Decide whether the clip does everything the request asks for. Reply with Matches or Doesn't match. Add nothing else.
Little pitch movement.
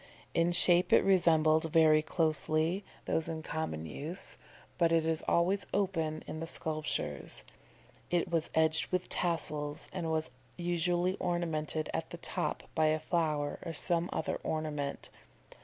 Matches